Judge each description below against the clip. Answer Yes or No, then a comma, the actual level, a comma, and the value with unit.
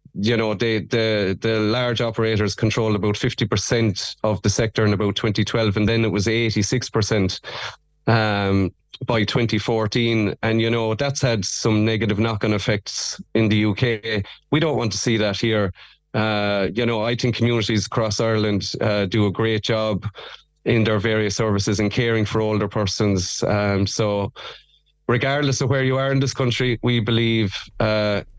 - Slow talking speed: No, average, 175 wpm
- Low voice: Yes, low, 110 Hz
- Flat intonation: Yes, narrow, 2.0 semitones